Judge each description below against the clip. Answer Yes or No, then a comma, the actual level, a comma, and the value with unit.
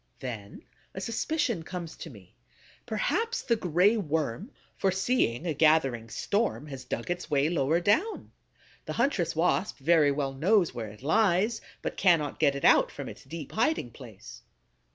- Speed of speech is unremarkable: Yes, average, 155 wpm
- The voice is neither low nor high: Yes, medium, 165 Hz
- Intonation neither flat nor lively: No, wide, 6.8 semitones